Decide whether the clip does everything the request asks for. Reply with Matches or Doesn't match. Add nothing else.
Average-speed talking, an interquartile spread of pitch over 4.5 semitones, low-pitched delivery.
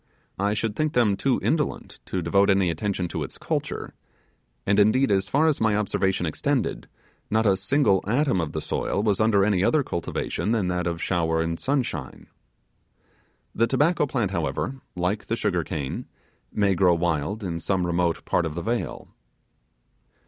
Doesn't match